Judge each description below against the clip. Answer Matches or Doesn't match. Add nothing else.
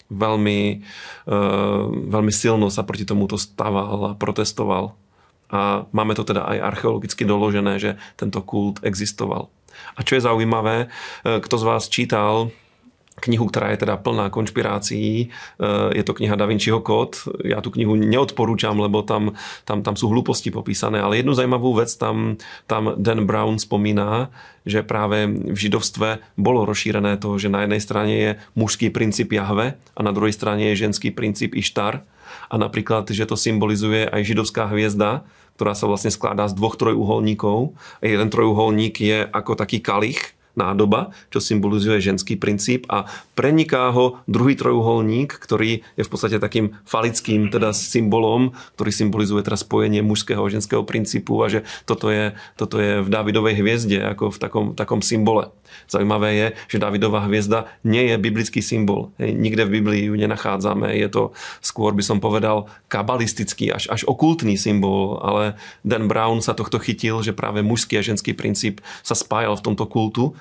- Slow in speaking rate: Doesn't match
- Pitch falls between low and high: Doesn't match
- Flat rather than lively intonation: Matches